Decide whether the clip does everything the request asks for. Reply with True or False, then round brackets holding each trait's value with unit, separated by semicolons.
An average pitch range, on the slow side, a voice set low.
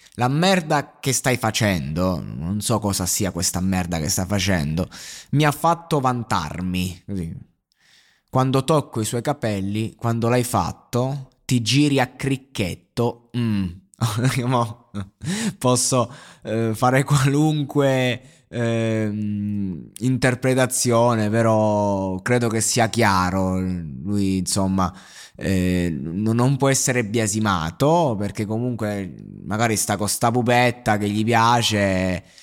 True (4.5 semitones; 110 wpm; 115 Hz)